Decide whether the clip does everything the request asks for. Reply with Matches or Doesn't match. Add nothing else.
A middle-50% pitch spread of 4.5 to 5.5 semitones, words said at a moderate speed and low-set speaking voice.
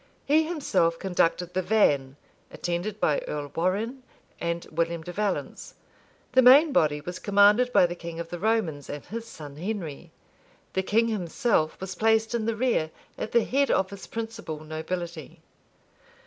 Doesn't match